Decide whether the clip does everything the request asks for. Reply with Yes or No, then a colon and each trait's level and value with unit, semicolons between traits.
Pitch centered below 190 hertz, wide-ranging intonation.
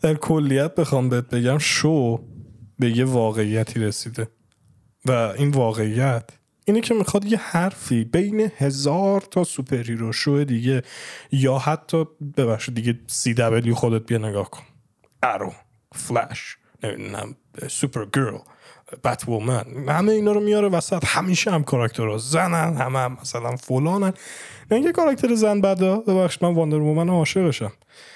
Yes: low, 135 Hz; wide, 6.4 semitones